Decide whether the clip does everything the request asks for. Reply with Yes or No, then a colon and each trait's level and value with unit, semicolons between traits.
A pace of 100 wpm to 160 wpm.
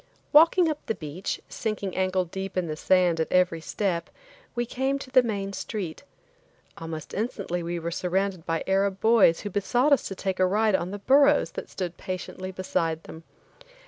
No: average, 180 wpm